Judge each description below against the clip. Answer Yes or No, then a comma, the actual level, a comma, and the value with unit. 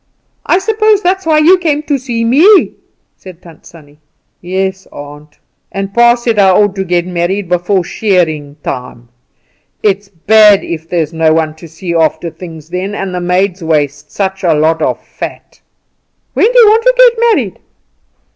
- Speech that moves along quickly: No, average, 170 wpm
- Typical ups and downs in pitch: No, wide, 6.5 semitones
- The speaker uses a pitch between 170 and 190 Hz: Yes, medium, 185 Hz